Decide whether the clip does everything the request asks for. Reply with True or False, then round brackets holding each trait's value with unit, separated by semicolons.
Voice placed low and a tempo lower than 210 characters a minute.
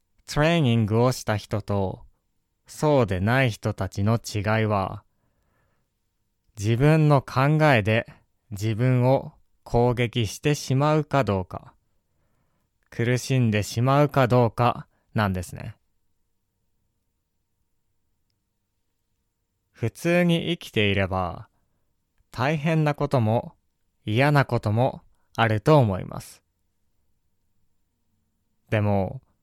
True (110 Hz; 180 characters per minute)